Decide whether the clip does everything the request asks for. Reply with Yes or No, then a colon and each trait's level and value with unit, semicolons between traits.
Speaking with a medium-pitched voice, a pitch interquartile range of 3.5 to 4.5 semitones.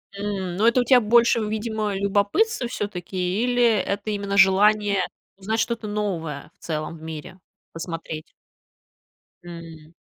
No: high, 200 Hz; average, 3.8 semitones